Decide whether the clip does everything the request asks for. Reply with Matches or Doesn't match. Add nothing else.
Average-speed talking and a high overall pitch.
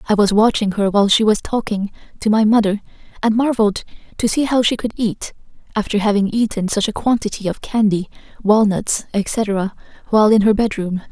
Matches